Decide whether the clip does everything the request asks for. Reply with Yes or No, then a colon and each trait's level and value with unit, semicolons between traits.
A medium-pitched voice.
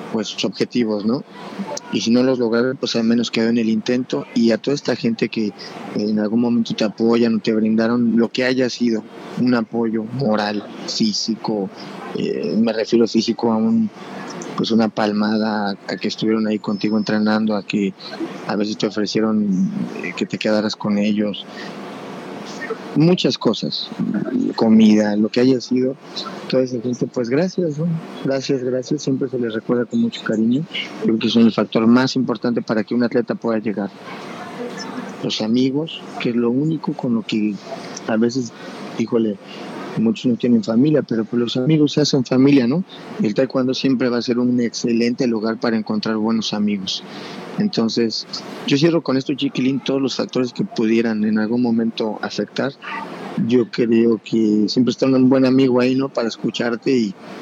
No: low, 120 Hz